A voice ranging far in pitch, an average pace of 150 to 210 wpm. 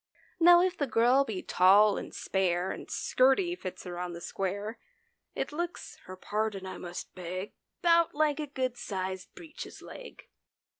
Yes: wide, 8.2 semitones; average, 160 wpm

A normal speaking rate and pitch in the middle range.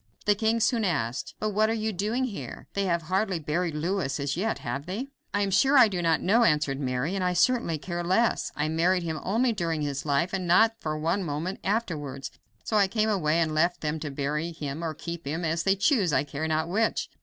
No: fast, 230 wpm; medium, 175 Hz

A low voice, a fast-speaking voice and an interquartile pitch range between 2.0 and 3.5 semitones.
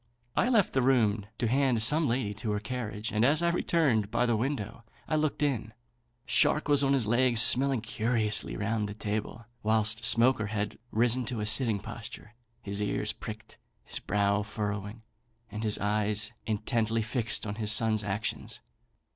No: low, 110 Hz; average, 170 wpm; average, 3.2 semitones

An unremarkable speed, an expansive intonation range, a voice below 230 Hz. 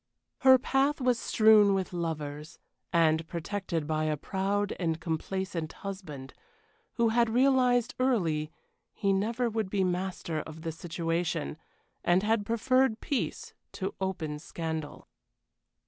No: slow, 125 wpm; wide, 5.7 semitones; high, 190 Hz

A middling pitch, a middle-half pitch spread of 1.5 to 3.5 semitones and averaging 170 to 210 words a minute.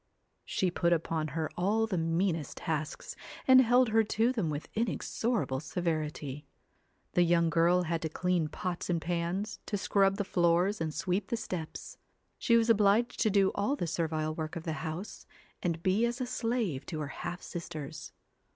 No: medium, 175 Hz; average, 4.6 semitones; average, 175 wpm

